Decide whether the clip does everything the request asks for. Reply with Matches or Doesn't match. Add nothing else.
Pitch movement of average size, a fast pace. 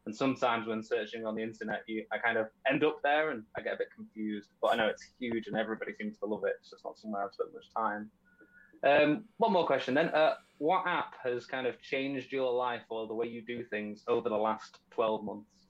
Doesn't match